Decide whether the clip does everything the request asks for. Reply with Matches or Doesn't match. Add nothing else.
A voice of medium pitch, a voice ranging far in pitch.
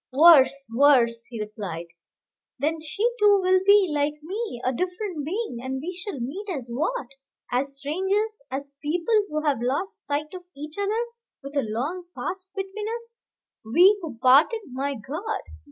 Doesn't match